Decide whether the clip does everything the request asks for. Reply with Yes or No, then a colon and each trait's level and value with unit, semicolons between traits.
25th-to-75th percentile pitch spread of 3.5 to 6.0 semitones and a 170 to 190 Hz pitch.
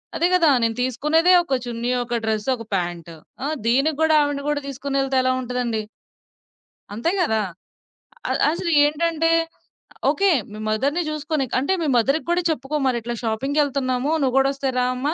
No: average, 4.2 semitones; very high, 270 Hz